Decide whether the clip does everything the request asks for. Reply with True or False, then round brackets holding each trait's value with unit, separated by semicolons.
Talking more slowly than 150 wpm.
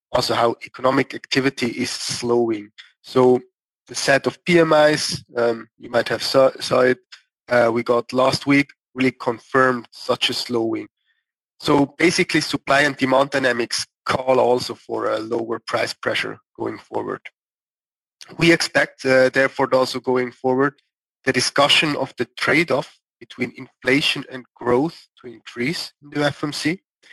True (140 wpm)